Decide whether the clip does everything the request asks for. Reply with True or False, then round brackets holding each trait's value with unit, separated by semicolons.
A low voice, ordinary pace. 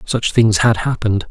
True (110 Hz; 185 wpm)